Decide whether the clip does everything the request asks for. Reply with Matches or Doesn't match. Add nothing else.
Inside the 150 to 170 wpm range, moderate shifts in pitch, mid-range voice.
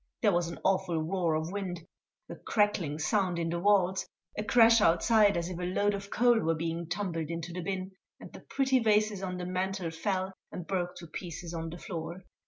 Doesn't match